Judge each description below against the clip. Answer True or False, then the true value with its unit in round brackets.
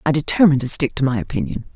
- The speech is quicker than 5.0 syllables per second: True (7.6 syllables/s)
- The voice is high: False (135 Hz)